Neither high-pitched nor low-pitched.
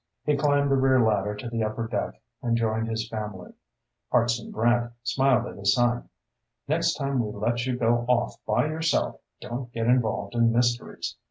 No: low, 120 Hz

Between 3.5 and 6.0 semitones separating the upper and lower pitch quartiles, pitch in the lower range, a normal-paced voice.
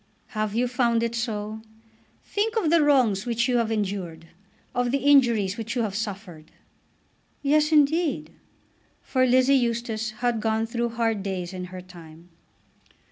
No: average, 3.8 semitones; high, 230 Hz; average, 150 wpm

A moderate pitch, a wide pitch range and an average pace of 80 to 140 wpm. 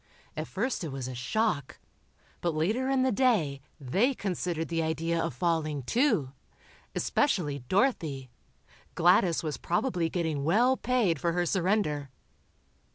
Yes: medium, 170 Hz; wide, 6.3 semitones; slow, 135 wpm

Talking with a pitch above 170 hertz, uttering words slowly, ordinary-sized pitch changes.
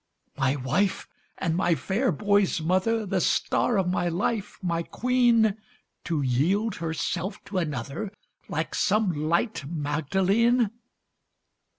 Yes: medium, 185 Hz; slow, 115 wpm; average, 4.8 semitones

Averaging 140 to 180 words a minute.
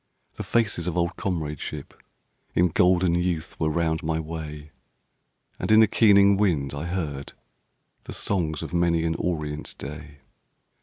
Yes: average, 145 wpm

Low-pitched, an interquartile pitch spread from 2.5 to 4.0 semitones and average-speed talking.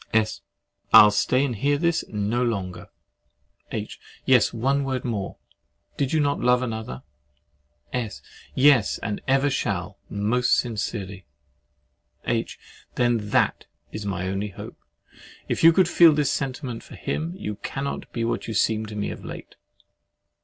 No: low, 120 Hz; average, 4.7 semitones; average, 145 wpm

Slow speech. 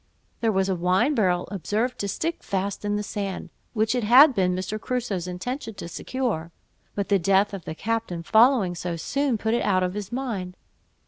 No: average, 195 wpm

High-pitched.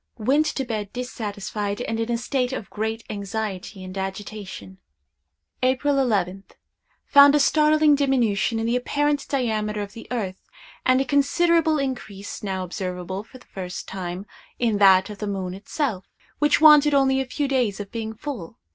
Yes: high, 225 Hz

